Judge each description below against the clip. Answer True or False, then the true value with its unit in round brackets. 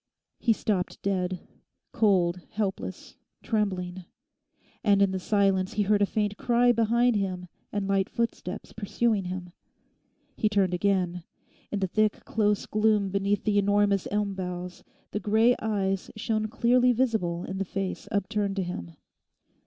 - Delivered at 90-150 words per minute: True (140 wpm)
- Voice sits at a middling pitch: False (200 Hz)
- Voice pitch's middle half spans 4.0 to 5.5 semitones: False (2.4 semitones)